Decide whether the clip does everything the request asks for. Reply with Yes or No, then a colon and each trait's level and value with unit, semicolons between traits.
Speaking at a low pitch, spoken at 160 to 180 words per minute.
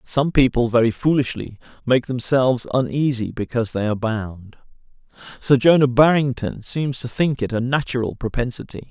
No: low, 125 Hz; average, 140 wpm